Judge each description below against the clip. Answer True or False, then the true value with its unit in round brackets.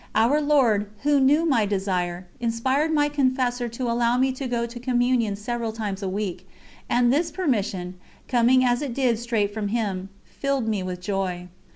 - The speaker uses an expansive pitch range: False (4.2 semitones)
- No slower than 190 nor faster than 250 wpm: False (175 wpm)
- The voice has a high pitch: True (235 Hz)